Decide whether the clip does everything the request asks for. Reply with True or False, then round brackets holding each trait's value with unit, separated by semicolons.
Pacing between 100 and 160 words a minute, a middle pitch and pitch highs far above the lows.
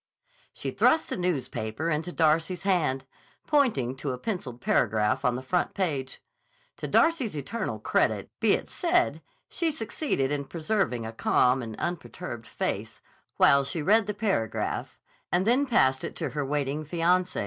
True (155 wpm; 160 Hz; 7.2 semitones)